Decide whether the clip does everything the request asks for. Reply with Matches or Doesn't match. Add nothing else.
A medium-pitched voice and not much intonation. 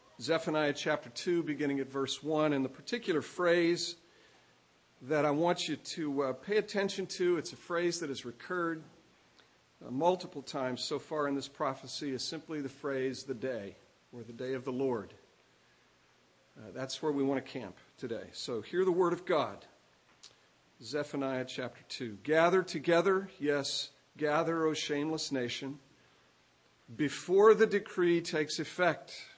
Doesn't match